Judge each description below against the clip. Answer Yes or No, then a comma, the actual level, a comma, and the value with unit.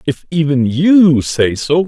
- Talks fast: No, average, 160 wpm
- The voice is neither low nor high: Yes, medium, 150 Hz